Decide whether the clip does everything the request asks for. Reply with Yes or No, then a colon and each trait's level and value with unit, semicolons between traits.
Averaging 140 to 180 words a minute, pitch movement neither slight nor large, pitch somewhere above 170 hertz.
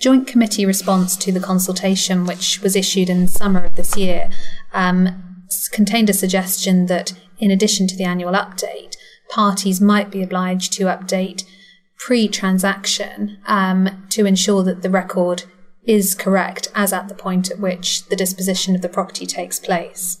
No: average, 160 wpm; narrow, 1.6 semitones; high, 190 Hz